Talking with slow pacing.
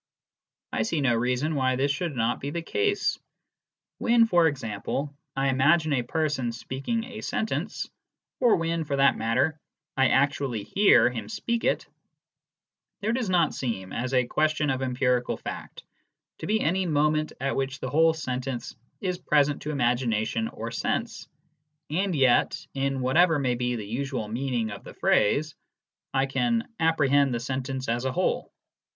No: average, 160 wpm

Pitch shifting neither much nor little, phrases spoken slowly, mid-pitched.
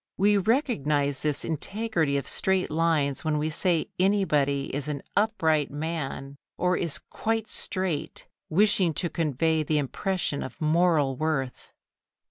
Yes: average, 4.4 semitones; slow, 130 wpm; medium, 160 Hz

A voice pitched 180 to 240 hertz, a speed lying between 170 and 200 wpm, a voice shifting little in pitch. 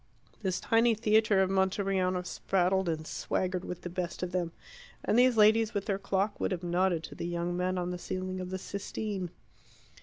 Yes: medium, 185 Hz; average, 190 wpm; narrow, 2.0 semitones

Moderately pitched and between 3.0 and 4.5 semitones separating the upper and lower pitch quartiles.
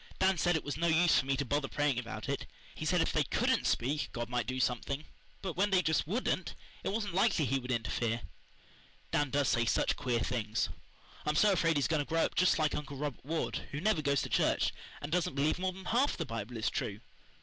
No: medium, 145 Hz; average, 5.2 semitones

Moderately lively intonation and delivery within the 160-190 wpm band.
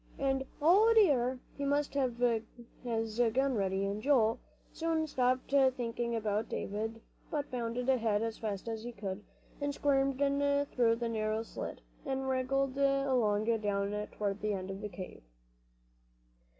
No: average, 4.2 semitones; average, 150 wpm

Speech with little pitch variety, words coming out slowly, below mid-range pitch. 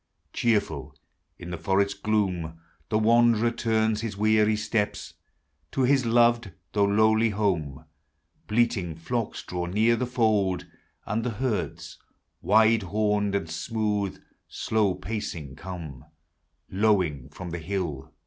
No: average, 3.6 semitones; slow, 120 wpm; low, 105 Hz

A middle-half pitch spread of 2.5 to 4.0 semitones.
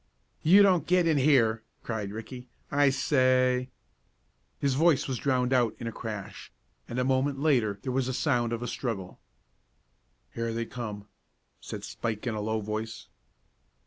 Yes: average, 3.5 semitones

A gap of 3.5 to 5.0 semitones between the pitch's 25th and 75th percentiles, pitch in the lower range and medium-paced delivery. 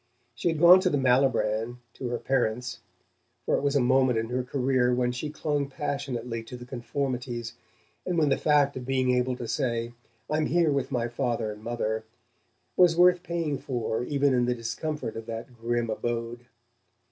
No: average, 3.1 semitones; low, 125 Hz; average, 180 wpm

